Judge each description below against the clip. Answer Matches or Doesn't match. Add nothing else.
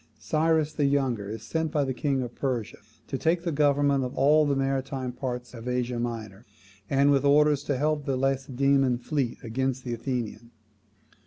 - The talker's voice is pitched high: Doesn't match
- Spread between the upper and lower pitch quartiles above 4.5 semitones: Doesn't match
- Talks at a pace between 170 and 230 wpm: Matches